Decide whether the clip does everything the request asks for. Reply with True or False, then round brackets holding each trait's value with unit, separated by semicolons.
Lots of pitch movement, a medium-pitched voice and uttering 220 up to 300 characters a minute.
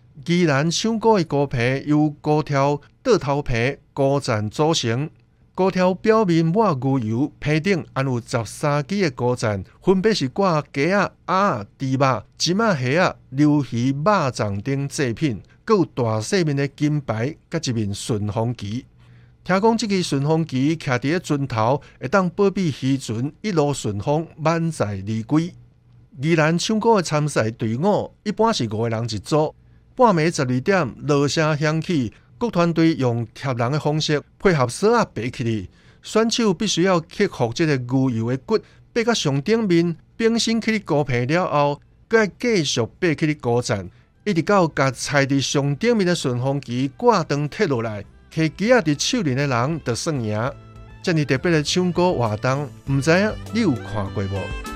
True (5.9 semitones; 145 Hz; 235 characters per minute)